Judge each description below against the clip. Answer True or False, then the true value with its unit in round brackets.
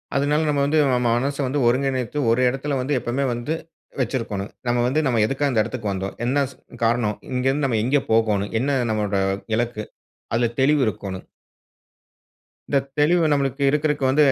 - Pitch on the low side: True (130 Hz)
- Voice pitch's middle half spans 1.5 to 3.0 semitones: False (3.8 semitones)